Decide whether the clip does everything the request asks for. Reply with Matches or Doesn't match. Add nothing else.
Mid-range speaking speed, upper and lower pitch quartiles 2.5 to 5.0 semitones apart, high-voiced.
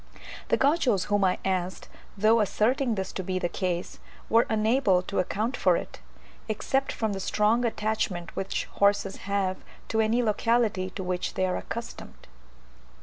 Matches